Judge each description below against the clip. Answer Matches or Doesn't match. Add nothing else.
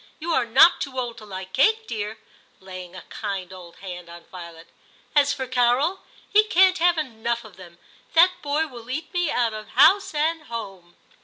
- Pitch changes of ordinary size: Doesn't match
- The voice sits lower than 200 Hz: Doesn't match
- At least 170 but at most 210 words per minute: Matches